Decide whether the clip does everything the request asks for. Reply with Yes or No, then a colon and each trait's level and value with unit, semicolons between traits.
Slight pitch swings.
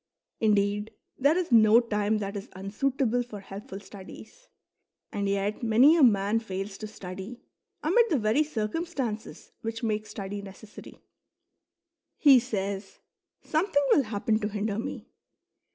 No: average, 3.5 semitones